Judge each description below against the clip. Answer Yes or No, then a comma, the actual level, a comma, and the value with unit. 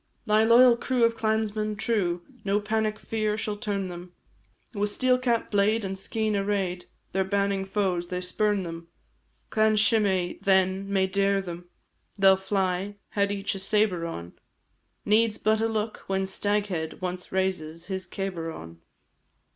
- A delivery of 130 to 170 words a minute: Yes, average, 155 wpm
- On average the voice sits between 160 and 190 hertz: No, high, 200 Hz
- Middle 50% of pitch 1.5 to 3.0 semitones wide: Yes, narrow, 2.5 semitones